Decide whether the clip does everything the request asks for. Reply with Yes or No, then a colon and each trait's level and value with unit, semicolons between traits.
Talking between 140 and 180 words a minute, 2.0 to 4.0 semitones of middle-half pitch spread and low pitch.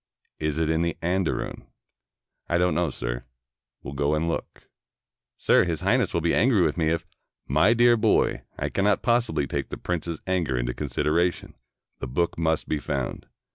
Yes: average, 175 wpm; average, 2.8 semitones; very low, 85 Hz